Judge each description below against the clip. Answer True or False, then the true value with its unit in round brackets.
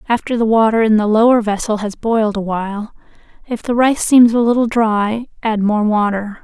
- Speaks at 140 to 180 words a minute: False (195 wpm)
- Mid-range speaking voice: False (220 Hz)